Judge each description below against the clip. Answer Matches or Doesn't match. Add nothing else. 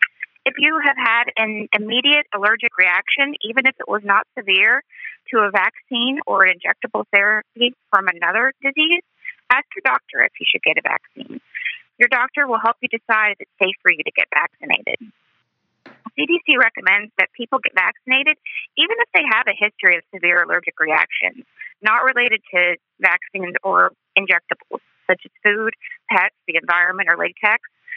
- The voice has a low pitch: Doesn't match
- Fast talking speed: Doesn't match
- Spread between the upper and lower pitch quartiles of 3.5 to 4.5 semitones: Doesn't match